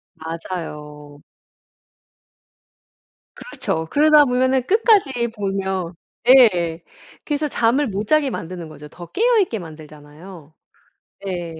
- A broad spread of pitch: Yes, wide, 8.5 semitones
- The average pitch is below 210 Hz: Yes, high, 190 Hz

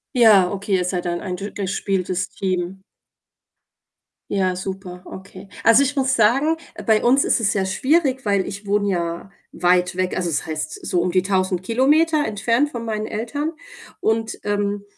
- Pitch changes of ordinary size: Yes, average, 3.8 semitones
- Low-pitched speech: No, high, 200 Hz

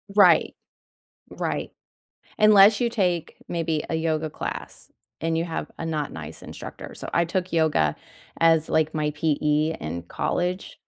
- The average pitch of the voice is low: No, medium, 160 Hz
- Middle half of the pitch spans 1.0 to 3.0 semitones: Yes, narrow, 2.5 semitones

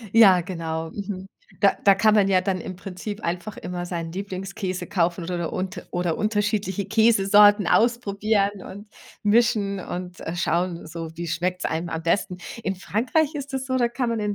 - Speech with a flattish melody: No, average, 3.1 semitones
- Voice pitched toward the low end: No, high, 195 Hz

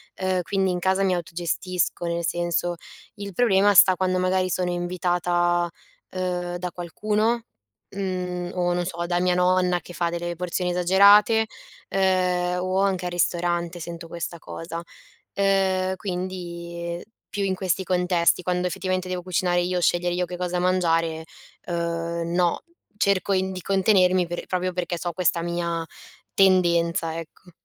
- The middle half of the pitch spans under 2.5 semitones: Yes, narrow, 1.3 semitones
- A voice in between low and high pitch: Yes, medium, 180 Hz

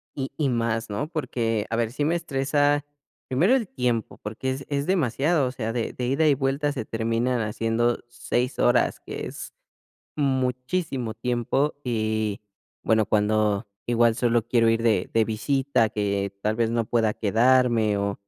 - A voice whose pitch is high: No, low, 120 Hz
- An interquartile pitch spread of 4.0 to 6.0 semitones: No, average, 3.3 semitones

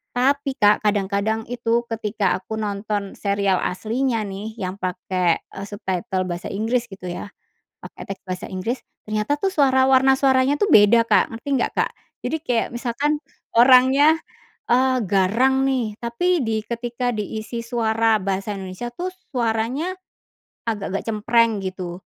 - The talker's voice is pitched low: No, high, 225 Hz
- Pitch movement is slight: No, average, 4.3 semitones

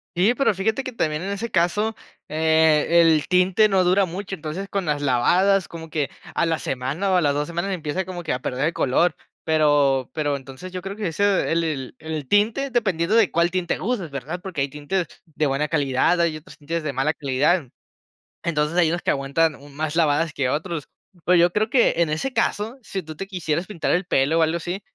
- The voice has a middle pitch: Yes, medium, 165 Hz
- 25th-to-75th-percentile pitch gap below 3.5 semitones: No, average, 4.1 semitones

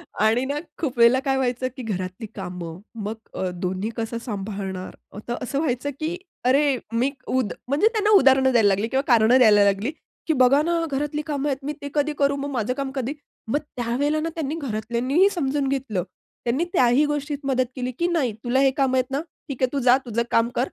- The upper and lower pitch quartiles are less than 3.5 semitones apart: No, average, 3.8 semitones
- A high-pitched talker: Yes, very high, 260 Hz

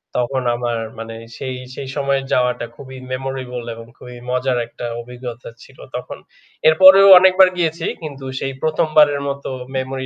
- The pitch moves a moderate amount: Yes, average, 3.2 semitones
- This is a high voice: No, low, 135 Hz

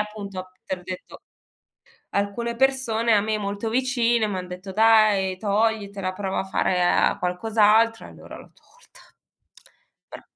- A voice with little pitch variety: No, average, 3.0 semitones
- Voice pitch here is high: Yes, high, 210 Hz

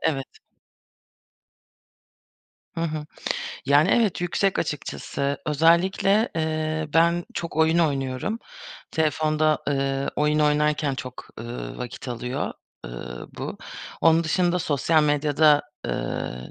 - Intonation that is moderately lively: Yes, average, 3.0 semitones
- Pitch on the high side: No, medium, 150 Hz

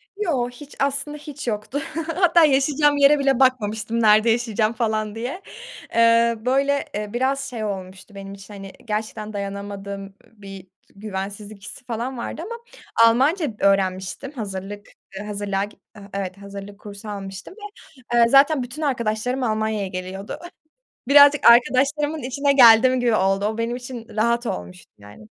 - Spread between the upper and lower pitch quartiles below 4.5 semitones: No, average, 4.9 semitones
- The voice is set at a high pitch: Yes, high, 225 Hz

